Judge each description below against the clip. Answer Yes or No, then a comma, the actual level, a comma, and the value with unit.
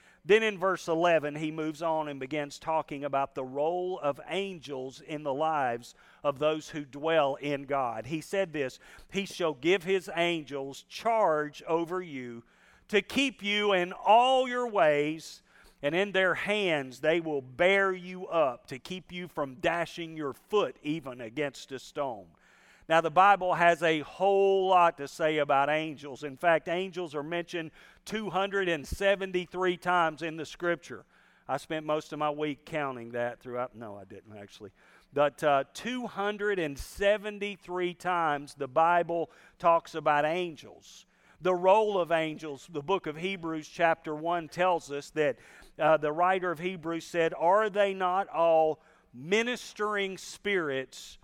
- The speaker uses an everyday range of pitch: Yes, average, 4.0 semitones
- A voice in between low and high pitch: Yes, medium, 165 Hz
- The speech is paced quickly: No, average, 150 wpm